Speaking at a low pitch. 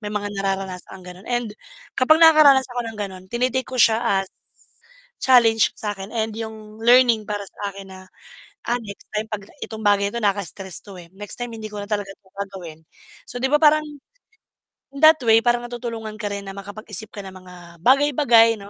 No: high, 215 Hz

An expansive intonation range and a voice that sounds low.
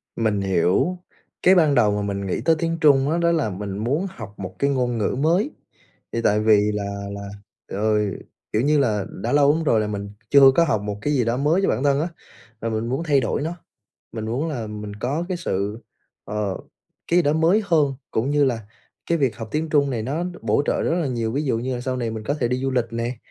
Yes: wide, 5.7 semitones; low, 125 Hz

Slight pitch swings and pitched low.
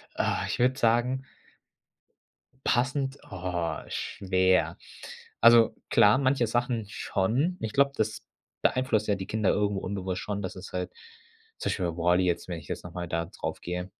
No: average, 4.8 semitones; low, 105 Hz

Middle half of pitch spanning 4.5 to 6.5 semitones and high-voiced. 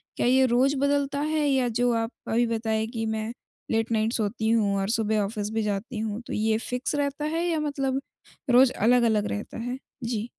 No: average, 3.3 semitones; high, 235 Hz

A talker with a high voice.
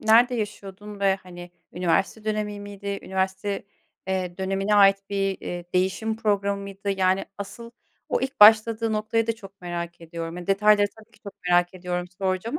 Yes: high, 195 Hz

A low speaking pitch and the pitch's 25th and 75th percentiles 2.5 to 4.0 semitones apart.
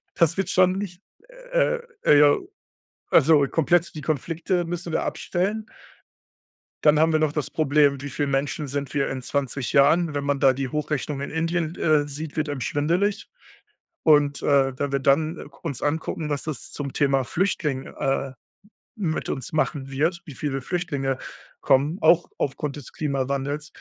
No: medium, 150 Hz; average, 2.8 semitones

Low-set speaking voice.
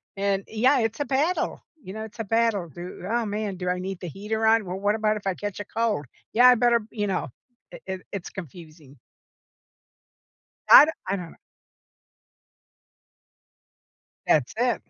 No: high, 205 Hz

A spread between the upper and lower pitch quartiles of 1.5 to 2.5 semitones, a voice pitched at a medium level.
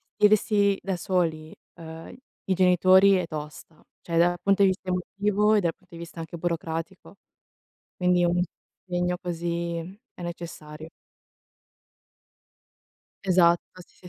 Yes: narrow, 2.0 semitones; medium, 175 Hz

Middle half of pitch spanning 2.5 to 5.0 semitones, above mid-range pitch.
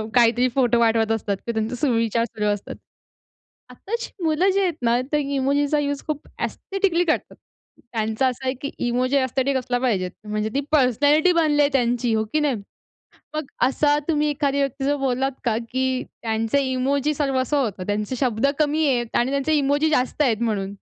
Yes: average, 3.8 semitones; very high, 260 Hz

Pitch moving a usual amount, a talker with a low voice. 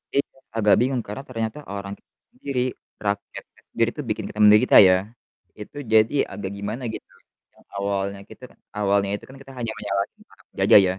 Yes: average, 3.4 semitones; low, 105 Hz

